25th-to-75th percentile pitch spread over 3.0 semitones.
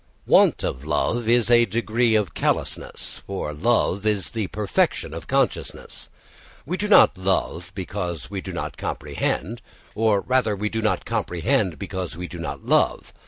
Yes: average, 4.4 semitones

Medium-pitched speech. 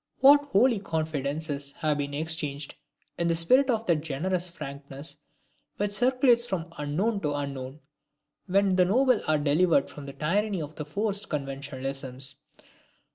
Yes: medium, 160 Hz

